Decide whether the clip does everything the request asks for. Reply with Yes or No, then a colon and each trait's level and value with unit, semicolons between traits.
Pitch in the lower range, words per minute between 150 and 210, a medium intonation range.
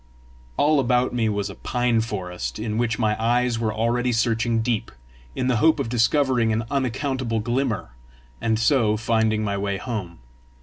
No: low, 115 Hz; average, 165 wpm; narrow, 2.2 semitones